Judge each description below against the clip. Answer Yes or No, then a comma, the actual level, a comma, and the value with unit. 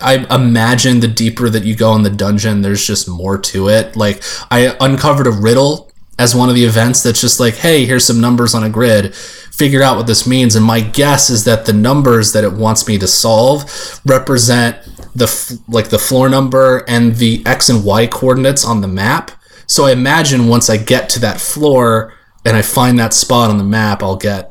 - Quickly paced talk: Yes, fast, 215 wpm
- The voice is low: Yes, low, 115 Hz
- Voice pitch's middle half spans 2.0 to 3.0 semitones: Yes, average, 2.7 semitones